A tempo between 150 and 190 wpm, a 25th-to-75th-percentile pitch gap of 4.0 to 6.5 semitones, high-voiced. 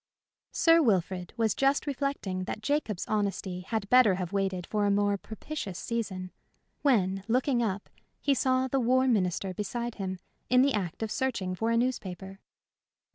Yes: average, 160 wpm; average, 5.1 semitones; high, 215 Hz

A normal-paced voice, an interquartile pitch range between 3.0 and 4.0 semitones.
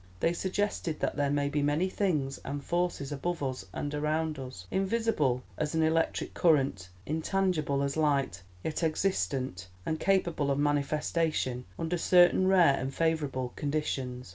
Yes: average, 145 wpm; average, 3.5 semitones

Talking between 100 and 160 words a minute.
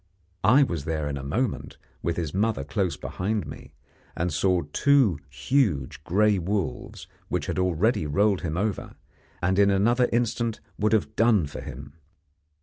Yes: average, 155 wpm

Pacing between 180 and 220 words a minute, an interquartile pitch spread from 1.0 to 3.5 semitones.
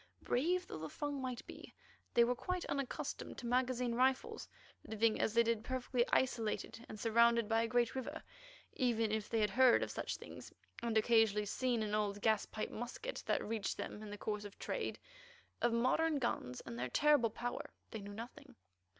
Yes: average, 185 wpm; average, 3.0 semitones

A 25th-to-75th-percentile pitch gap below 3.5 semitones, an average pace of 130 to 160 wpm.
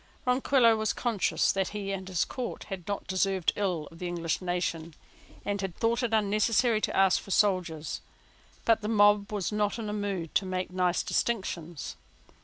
No: average, 2.9 semitones; average, 170 wpm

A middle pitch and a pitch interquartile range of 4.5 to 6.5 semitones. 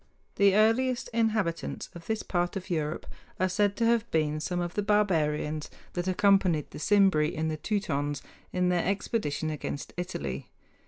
Yes: medium, 180 Hz; average, 4.9 semitones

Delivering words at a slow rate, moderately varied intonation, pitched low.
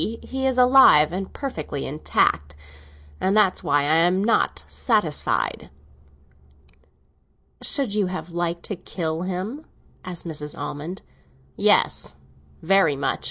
No: slow, 115 wpm; average, 5.0 semitones; medium, 180 Hz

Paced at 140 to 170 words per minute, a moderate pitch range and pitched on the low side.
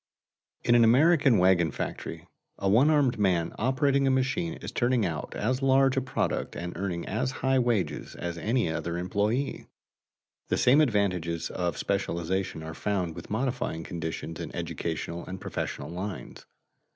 No: average, 150 wpm; wide, 7.1 semitones; low, 105 Hz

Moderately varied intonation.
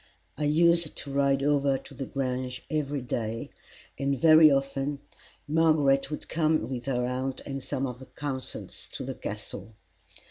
No: narrow, 2.3 semitones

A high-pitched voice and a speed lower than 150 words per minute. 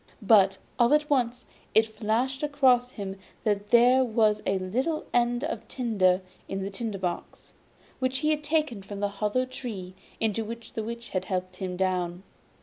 No: high, 225 Hz; average, 170 wpm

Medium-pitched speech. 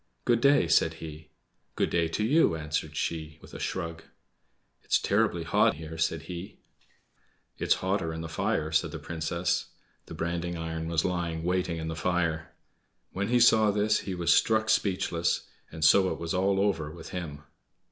No: very low, 85 Hz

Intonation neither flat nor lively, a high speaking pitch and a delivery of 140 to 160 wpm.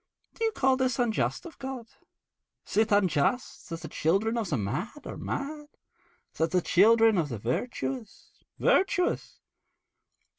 No: wide, 7.3 semitones; high, 225 Hz; average, 145 wpm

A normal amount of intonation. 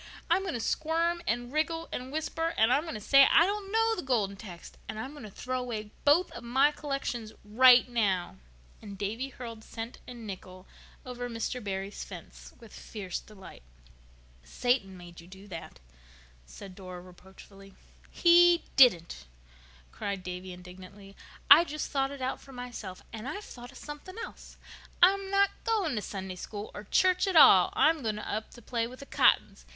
No: wide, 7.0 semitones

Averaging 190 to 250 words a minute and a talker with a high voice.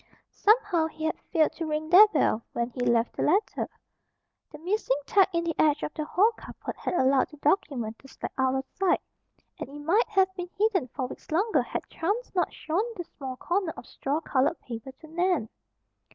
Yes: average, 200 wpm; very high, 315 Hz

